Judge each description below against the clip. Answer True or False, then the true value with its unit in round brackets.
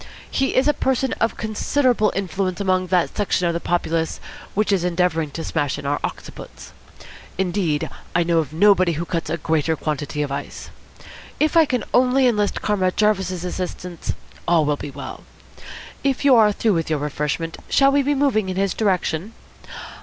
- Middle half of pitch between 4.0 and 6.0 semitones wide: True (4.8 semitones)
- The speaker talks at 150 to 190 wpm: True (175 wpm)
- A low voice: False (185 Hz)